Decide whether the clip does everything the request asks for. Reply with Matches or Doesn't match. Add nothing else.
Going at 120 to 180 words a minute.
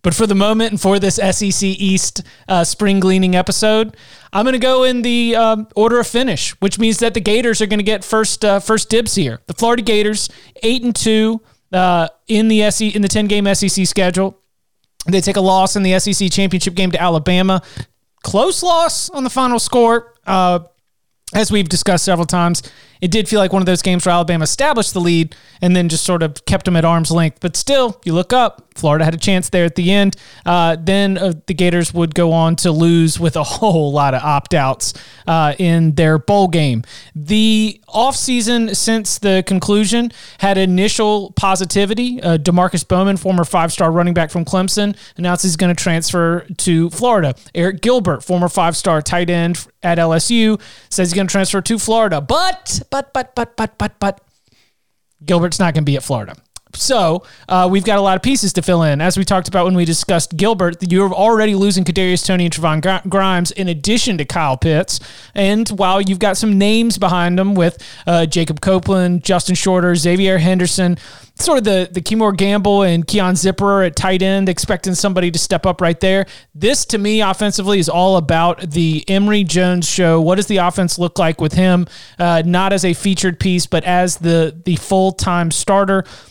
Doesn't match